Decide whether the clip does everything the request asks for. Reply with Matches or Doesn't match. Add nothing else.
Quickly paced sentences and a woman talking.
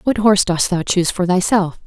Matches